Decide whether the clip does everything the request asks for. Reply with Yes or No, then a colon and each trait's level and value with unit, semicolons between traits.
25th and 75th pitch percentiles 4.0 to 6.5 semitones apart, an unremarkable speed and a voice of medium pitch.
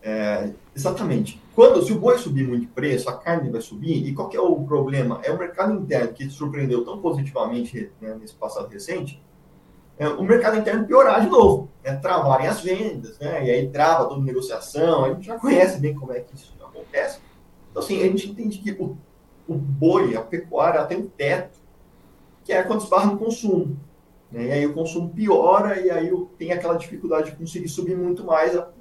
No: wide, 5.4 semitones; fast, 205 wpm; medium, 165 Hz